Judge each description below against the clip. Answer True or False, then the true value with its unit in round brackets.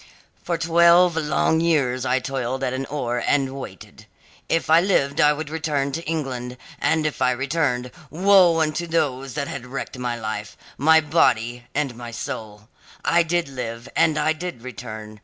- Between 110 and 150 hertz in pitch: True (140 Hz)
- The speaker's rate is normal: True (170 wpm)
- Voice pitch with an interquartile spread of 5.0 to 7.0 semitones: False (4.4 semitones)